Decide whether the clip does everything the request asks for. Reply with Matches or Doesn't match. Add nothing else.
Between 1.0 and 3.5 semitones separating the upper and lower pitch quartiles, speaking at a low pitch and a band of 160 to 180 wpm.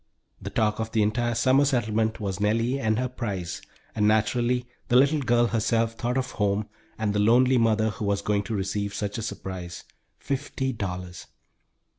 Matches